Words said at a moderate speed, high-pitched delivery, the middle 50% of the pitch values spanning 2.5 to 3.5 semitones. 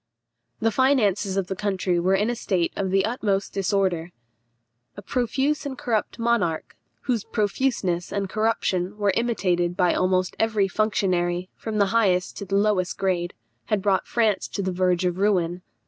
Yes: average, 160 wpm; high, 195 Hz; average, 3.1 semitones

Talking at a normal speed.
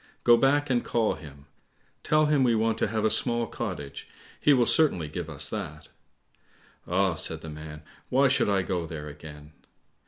Yes: average, 180 wpm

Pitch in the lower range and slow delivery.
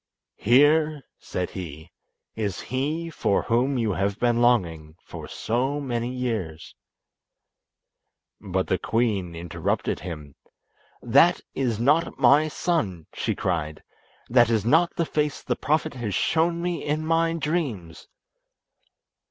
Yes: low, 120 Hz; slow, 120 wpm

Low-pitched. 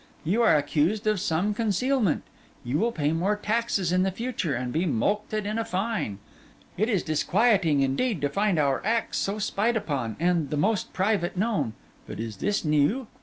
No: high, 190 Hz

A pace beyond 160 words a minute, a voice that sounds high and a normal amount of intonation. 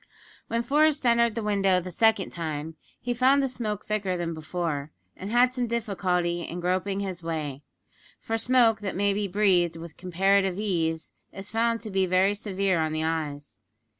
Yes: average, 175 wpm; high, 195 Hz; average, 4.6 semitones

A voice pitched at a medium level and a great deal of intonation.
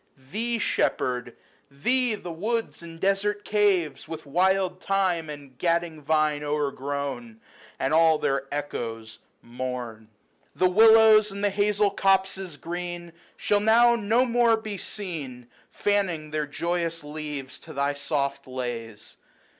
Yes: medium, 165 Hz; wide, 6.2 semitones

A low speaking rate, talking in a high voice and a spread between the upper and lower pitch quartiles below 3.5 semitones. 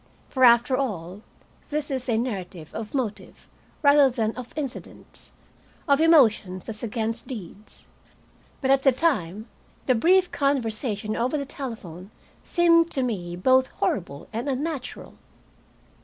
No: slow, 130 wpm; high, 245 Hz; average, 4.7 semitones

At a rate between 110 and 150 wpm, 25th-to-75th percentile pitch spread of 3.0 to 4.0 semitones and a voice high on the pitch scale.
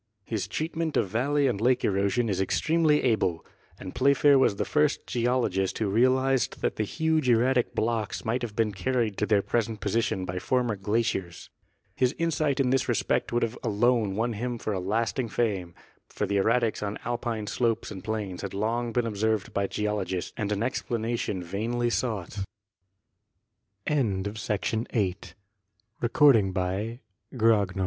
No: average, 145 wpm; average, 3.6 semitones; low, 115 Hz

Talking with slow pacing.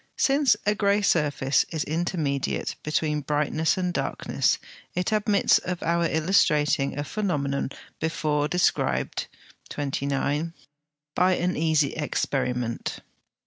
Yes: slow, 105 wpm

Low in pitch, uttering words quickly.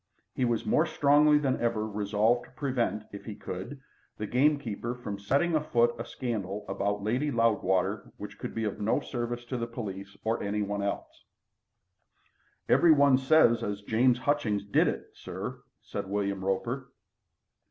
No: low, 115 Hz; average, 155 wpm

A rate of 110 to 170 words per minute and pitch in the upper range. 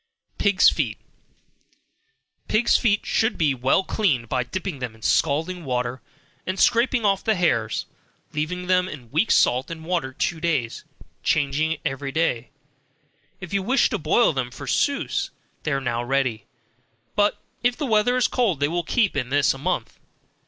No: average, 165 wpm; medium, 160 Hz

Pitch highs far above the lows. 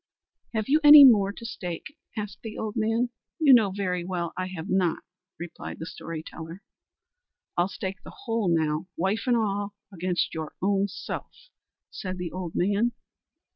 No: average, 4.0 semitones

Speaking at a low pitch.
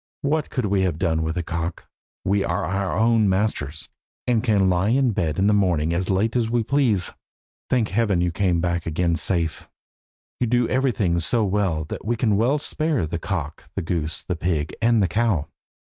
Yes: very low, 95 Hz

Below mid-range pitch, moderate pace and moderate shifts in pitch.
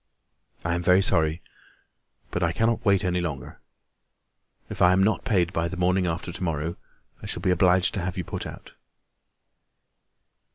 No: very low, 90 Hz; average, 170 wpm; narrow, 1.7 semitones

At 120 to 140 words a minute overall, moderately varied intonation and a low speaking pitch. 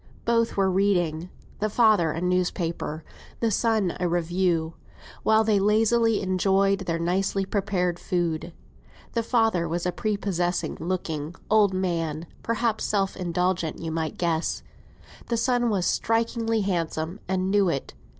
No: slow, 135 wpm; average, 3.8 semitones; medium, 185 Hz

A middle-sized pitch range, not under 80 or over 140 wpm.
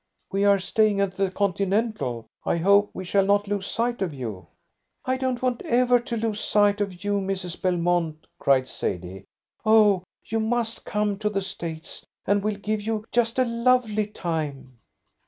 No: average, 3.6 semitones; average, 170 wpm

